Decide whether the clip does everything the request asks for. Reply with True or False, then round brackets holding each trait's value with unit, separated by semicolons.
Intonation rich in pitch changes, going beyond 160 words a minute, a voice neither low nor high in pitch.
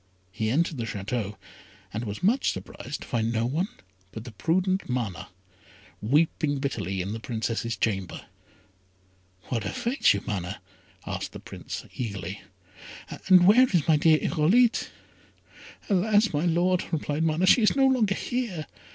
False (8.9 semitones; 145 wpm; 150 Hz)